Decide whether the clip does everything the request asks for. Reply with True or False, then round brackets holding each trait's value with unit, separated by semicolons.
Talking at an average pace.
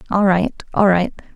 True (175 wpm)